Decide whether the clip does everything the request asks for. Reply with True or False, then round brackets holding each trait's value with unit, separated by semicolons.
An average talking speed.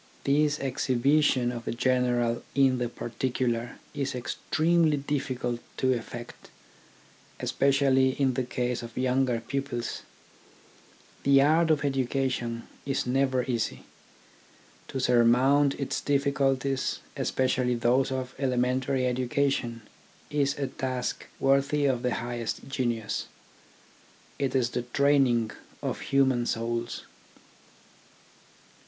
False (110 wpm)